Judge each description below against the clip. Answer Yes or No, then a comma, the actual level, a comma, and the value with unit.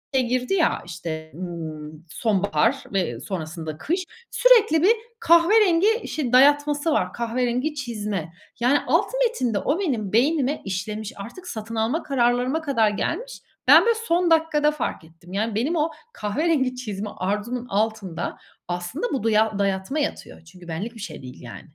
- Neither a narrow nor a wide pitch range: No, wide, 7.9 semitones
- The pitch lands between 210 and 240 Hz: Yes, high, 235 Hz